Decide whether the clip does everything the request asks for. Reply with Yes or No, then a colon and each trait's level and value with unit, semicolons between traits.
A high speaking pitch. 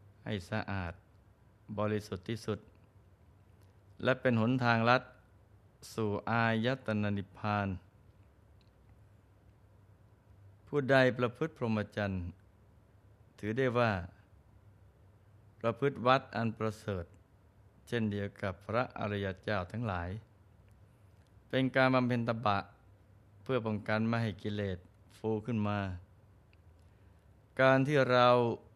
No: low, 105 Hz